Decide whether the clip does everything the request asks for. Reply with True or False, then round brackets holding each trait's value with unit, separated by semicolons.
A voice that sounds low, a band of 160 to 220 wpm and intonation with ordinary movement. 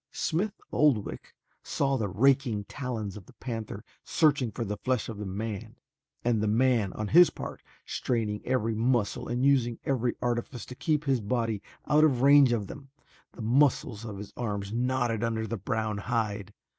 True (115 Hz; 170 wpm; 3.6 semitones)